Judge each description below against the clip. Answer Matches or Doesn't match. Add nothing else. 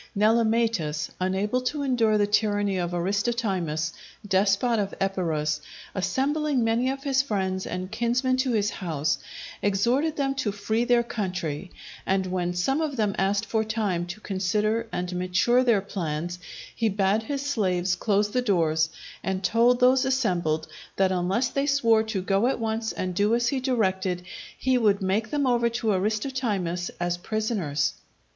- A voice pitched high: Matches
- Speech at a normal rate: Matches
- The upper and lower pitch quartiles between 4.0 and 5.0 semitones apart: Matches